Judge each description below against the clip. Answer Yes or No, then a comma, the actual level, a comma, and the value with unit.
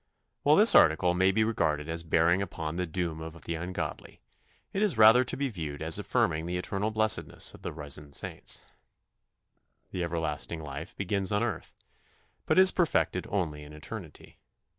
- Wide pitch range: No, average, 4.5 semitones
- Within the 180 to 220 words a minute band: No, average, 170 wpm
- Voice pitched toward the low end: Yes, very low, 85 Hz